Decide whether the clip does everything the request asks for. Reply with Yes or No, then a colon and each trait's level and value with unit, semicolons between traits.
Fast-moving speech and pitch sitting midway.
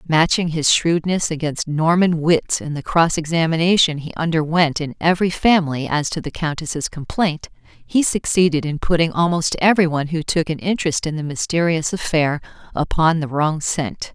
No: average, 160 wpm; medium, 160 Hz